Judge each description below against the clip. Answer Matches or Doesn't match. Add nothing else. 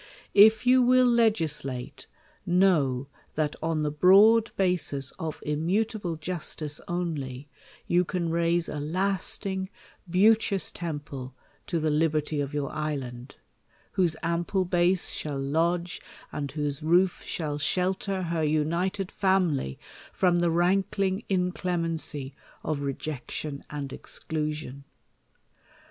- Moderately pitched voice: Matches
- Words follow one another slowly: Matches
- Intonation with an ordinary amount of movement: Matches